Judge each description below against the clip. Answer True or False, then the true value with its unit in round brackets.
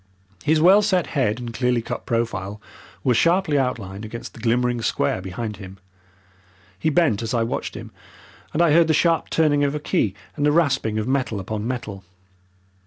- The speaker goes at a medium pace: True (180 wpm)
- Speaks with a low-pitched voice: True (125 Hz)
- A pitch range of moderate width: False (5.8 semitones)